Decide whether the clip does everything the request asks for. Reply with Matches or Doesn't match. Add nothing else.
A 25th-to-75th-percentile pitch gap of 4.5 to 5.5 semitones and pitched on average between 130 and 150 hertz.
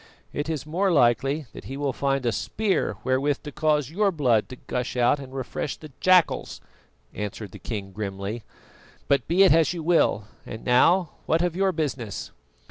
Matches